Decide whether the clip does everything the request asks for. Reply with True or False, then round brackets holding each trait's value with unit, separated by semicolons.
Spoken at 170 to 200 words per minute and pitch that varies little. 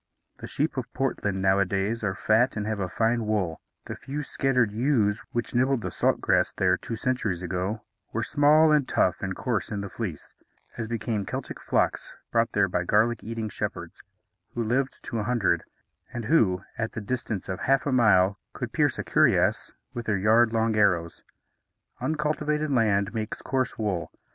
False (175 wpm; 4.1 semitones)